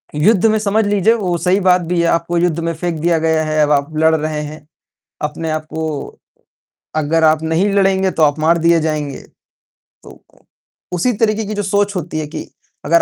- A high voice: No, medium, 165 Hz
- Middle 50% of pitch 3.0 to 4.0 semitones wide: Yes, average, 3.4 semitones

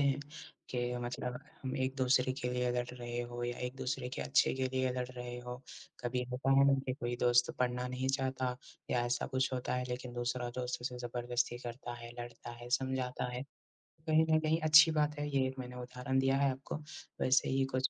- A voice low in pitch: Yes, low, 125 Hz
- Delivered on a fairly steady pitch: Yes, narrow, 1.3 semitones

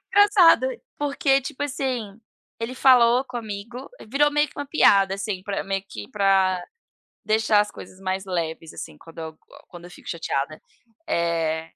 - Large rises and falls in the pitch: Yes, wide, 6.7 semitones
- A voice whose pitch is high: Yes, high, 200 Hz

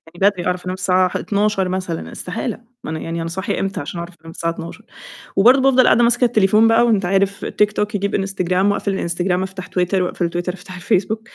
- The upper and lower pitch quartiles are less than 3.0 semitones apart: Yes, narrow, 2.6 semitones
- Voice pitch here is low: No, high, 190 Hz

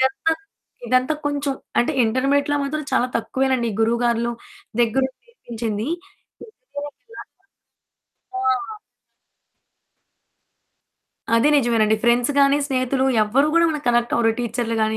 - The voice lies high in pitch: Yes, very high, 255 Hz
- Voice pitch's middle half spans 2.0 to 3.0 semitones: No, average, 3.4 semitones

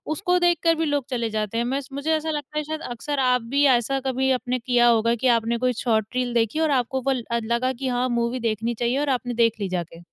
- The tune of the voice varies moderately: Yes, average, 3.2 semitones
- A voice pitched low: No, very high, 250 Hz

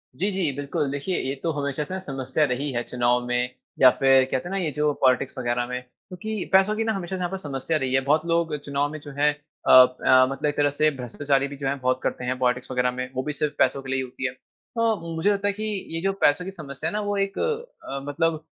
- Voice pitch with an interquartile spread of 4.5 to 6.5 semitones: Yes, average, 5.0 semitones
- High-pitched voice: No, medium, 145 Hz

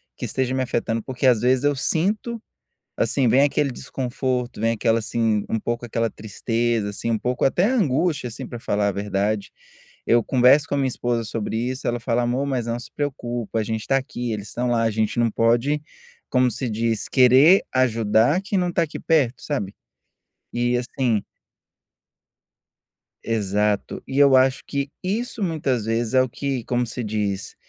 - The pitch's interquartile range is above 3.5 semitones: No, average, 3.0 semitones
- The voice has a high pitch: No, low, 120 Hz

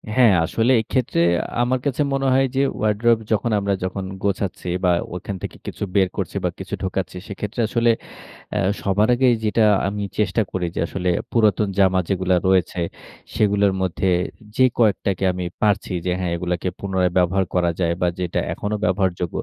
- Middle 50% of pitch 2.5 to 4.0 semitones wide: Yes, average, 2.9 semitones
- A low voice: Yes, low, 100 Hz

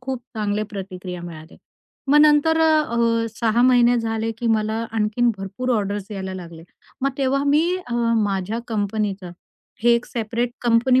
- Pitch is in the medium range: No, high, 225 Hz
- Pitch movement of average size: Yes, average, 3.5 semitones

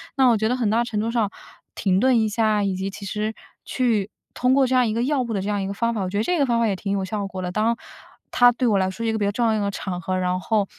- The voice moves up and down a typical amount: Yes, average, 3.1 semitones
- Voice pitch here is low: No, high, 215 Hz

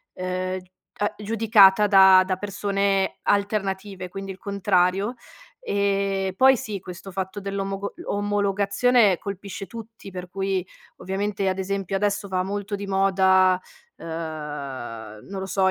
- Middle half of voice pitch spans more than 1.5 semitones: No, narrow, 1.2 semitones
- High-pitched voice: Yes, high, 195 Hz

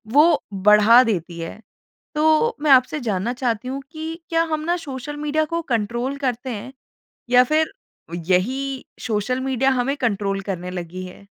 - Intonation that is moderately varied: No, wide, 6.1 semitones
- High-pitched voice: Yes, very high, 255 Hz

